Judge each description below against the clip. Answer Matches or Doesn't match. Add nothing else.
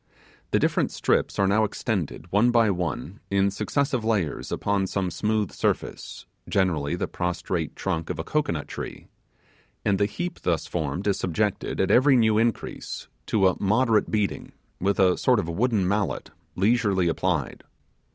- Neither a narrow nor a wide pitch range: Matches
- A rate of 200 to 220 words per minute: Doesn't match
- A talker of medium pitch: Doesn't match